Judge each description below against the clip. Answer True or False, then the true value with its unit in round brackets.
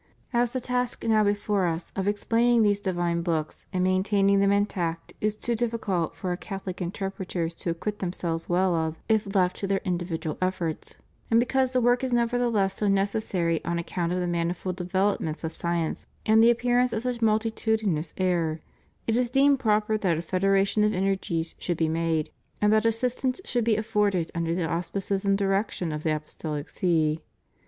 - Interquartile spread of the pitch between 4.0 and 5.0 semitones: True (4.3 semitones)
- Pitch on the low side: False (195 Hz)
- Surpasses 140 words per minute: True (185 wpm)